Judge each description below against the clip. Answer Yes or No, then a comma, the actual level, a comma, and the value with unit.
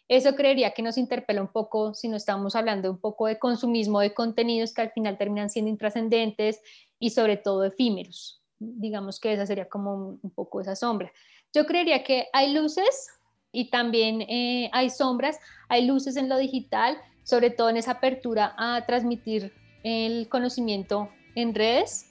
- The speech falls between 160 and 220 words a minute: Yes, average, 170 wpm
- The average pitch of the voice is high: Yes, high, 230 Hz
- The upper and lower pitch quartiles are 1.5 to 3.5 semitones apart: Yes, average, 2.8 semitones